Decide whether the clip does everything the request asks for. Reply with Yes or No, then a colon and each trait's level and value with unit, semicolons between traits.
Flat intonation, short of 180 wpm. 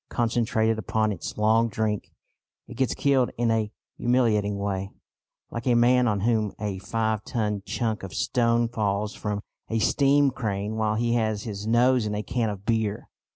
Yes: narrow, 2.1 semitones; average, 170 wpm